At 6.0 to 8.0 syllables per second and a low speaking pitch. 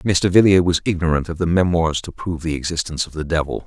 Yes: 6.4 syllables/s; very low, 85 Hz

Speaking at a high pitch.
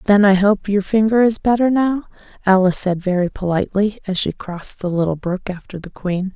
Yes: high, 195 Hz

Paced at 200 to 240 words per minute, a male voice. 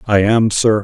Yes: fast, 215 wpm; male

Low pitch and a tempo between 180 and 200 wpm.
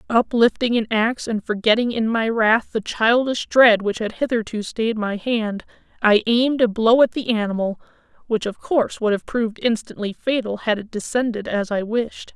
No: high, 225 Hz; average, 185 wpm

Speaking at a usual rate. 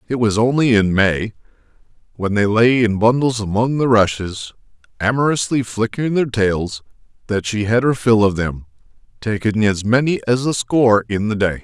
Yes: average, 170 wpm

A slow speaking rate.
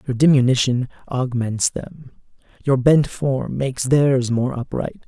Yes: slow, 130 wpm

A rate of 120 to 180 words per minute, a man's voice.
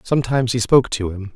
No: fast, 220 wpm; male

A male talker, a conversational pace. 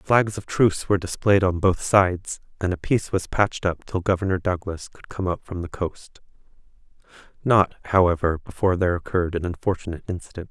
Yes: male; average, 175 wpm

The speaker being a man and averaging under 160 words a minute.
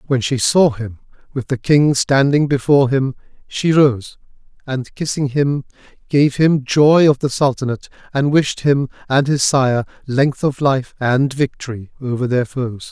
No: male; average, 165 wpm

